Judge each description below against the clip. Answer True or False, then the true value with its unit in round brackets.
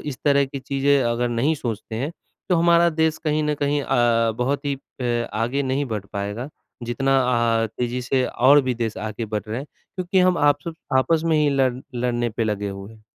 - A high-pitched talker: False (130 Hz)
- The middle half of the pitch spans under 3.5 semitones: False (3.8 semitones)